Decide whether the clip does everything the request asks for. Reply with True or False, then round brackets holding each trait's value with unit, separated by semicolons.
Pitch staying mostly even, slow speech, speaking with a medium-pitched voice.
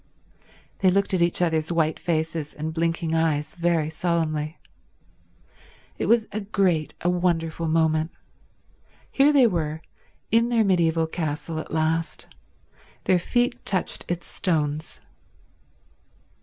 True (2.3 semitones; 120 wpm; 165 Hz)